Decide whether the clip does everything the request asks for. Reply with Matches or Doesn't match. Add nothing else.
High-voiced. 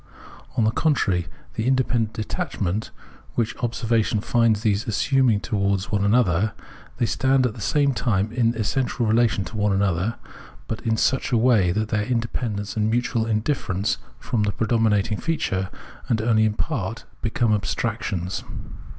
Doesn't match